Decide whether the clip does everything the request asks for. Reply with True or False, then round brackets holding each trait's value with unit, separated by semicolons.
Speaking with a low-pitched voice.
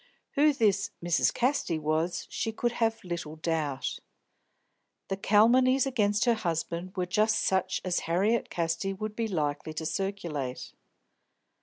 False (190 Hz)